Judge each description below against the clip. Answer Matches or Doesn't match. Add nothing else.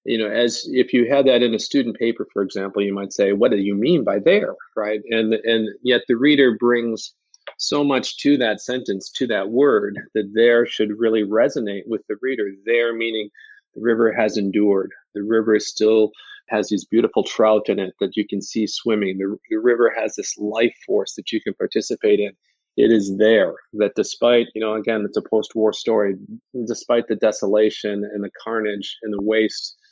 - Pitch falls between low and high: Doesn't match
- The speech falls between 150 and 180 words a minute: Doesn't match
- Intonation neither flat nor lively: Doesn't match